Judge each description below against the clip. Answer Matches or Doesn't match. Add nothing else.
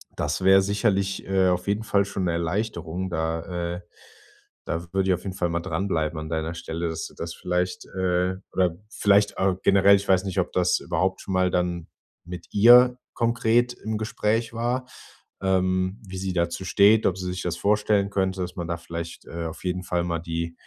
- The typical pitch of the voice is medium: Doesn't match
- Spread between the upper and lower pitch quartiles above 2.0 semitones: Matches